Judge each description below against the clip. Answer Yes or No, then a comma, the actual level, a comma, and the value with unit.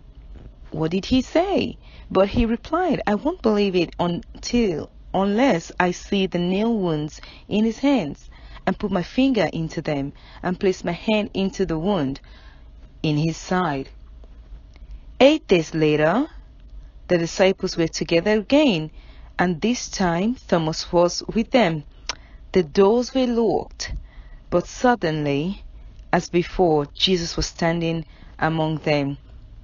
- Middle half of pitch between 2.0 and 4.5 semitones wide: No, average, 5.2 semitones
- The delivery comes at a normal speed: No, slow, 130 wpm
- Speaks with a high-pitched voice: No, medium, 180 Hz